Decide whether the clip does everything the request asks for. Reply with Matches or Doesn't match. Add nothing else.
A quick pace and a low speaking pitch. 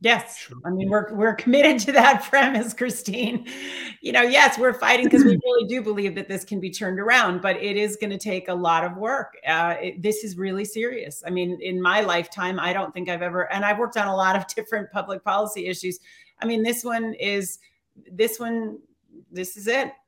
Doesn't match